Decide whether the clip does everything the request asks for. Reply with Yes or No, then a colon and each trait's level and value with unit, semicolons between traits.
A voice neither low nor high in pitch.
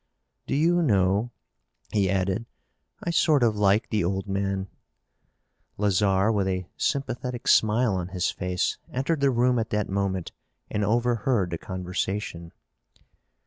No: low, 105 Hz